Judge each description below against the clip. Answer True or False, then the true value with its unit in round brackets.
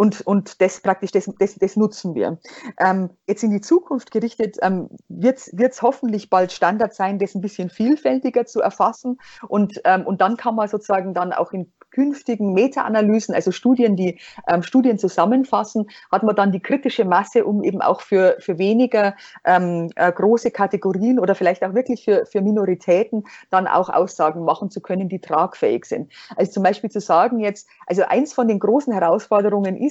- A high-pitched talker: True (205 Hz)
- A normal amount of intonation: True (3.7 semitones)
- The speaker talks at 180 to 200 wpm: True (185 wpm)